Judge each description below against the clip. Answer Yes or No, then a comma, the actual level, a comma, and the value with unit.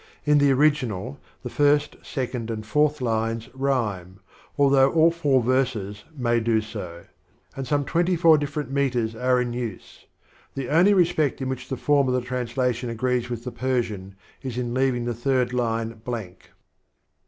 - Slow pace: No, average, 165 wpm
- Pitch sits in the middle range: No, low, 125 Hz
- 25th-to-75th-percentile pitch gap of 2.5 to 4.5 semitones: Yes, average, 3.4 semitones